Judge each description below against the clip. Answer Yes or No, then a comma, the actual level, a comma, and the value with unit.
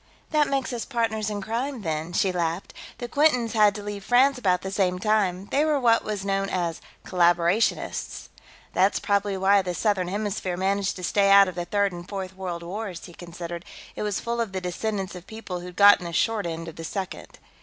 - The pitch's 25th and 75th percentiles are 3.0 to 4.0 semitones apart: Yes, average, 3.3 semitones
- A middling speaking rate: No, fast, 210 wpm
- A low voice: No, high, 195 Hz